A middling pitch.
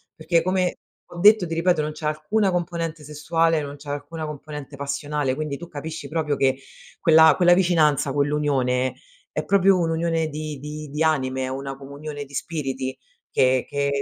Yes: medium, 150 Hz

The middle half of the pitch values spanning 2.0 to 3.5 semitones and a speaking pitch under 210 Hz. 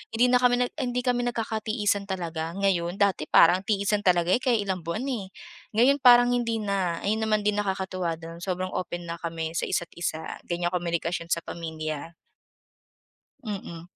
No: average, 4.5 semitones; high, 190 Hz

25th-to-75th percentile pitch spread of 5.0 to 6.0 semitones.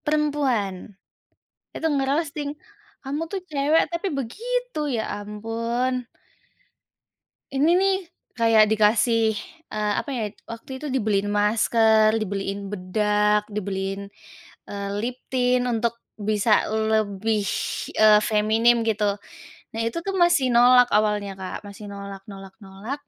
No: average, 4.1 semitones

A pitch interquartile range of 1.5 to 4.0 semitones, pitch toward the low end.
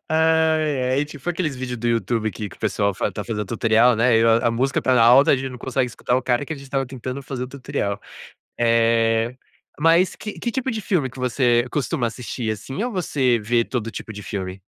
Yes: average, 3.5 semitones; low, 125 Hz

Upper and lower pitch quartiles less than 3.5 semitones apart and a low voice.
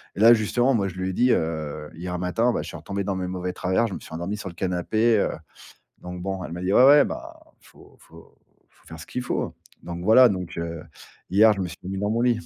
No: average, 3.8 semitones; very low, 95 Hz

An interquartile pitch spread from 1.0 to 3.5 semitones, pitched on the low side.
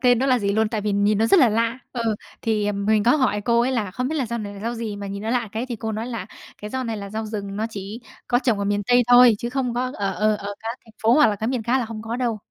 No: average, 2.8 semitones; high, 225 Hz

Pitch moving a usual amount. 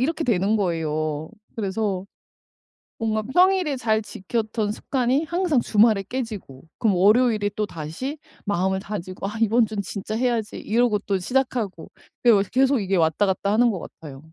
Yes: average, 4.2 semitones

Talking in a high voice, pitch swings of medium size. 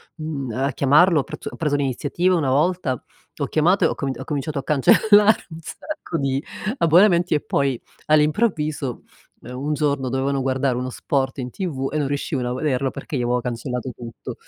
No: medium, 140 Hz; average, 3.3 semitones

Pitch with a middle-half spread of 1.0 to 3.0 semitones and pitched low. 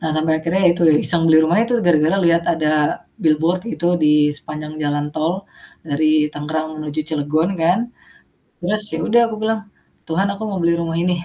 No: narrow, 2.4 semitones; medium, 165 Hz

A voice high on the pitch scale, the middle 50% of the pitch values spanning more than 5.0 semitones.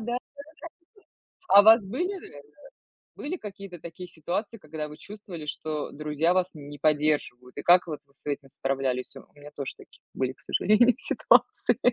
No: medium, 155 Hz; wide, 5.4 semitones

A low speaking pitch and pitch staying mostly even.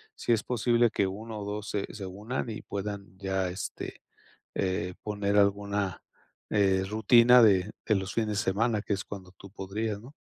Yes: low, 100 Hz; narrow, 2.1 semitones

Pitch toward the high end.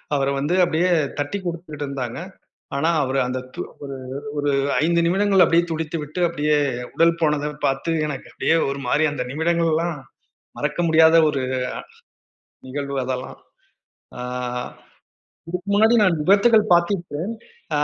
No: medium, 160 Hz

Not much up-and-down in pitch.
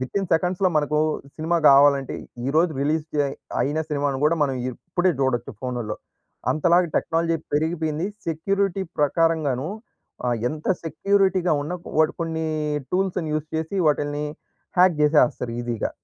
No: average, 3.2 semitones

